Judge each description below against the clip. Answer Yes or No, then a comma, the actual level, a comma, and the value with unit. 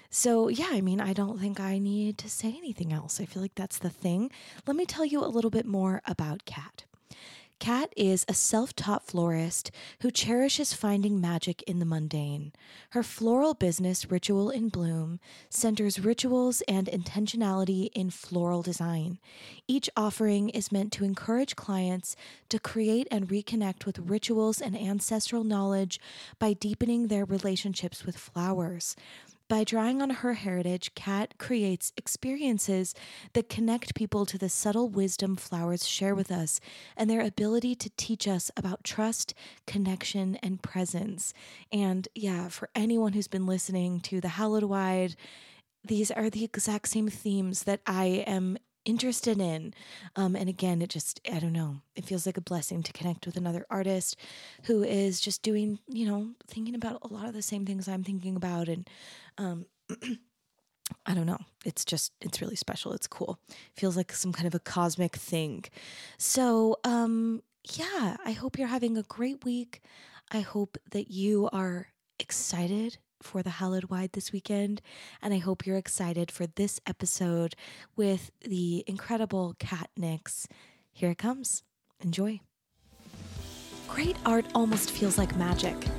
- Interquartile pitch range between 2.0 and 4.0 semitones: Yes, average, 3.4 semitones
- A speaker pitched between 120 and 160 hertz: No, high, 200 Hz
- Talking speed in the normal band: Yes, average, 160 wpm